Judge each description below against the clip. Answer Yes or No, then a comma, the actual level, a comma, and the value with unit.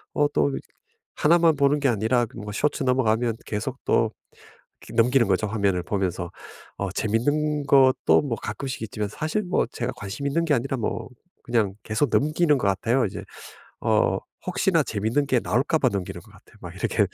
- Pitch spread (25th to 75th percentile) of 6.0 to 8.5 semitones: No, wide, 5.4 semitones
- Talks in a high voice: No, low, 120 Hz